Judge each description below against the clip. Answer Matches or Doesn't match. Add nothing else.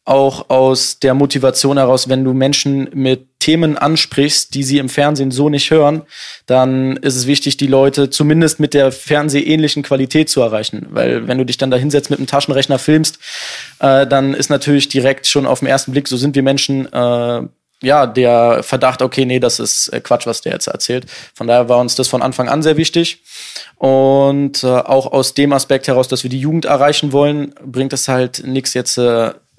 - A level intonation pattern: Matches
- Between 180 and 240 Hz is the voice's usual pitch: Doesn't match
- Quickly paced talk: Matches